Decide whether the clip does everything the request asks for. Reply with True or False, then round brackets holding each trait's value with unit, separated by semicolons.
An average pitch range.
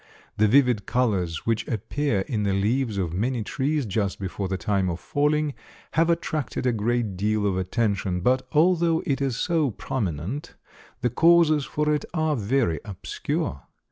False (6.6 semitones)